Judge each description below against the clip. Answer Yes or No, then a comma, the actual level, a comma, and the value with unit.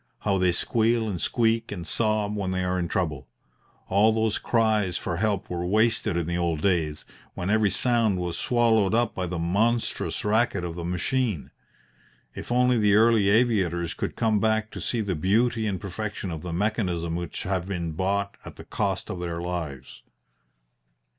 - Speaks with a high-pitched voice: No, low, 100 Hz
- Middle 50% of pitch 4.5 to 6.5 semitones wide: No, average, 4.1 semitones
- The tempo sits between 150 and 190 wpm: Yes, average, 180 wpm